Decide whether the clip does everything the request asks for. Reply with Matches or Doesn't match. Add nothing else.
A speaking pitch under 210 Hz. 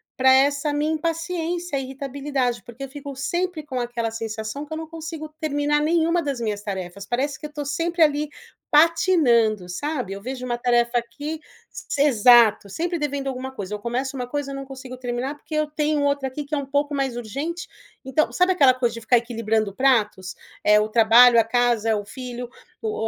Doesn't match